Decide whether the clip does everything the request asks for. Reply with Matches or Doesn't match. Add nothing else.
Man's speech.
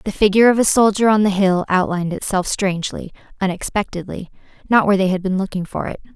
Doesn't match